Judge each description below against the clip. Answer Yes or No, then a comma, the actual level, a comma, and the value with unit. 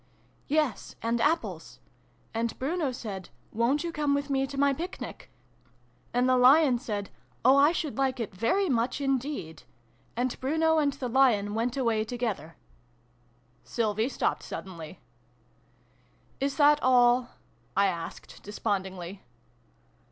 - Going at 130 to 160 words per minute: Yes, average, 150 wpm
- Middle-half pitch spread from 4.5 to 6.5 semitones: Yes, average, 5.3 semitones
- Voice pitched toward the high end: Yes, high, 245 Hz